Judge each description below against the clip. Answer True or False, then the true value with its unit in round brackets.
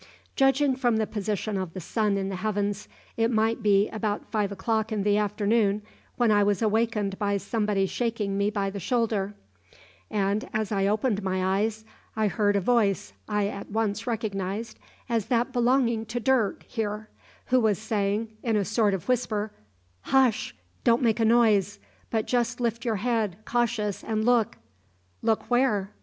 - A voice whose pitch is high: True (215 Hz)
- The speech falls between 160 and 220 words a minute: True (170 wpm)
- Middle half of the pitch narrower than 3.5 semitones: True (2.4 semitones)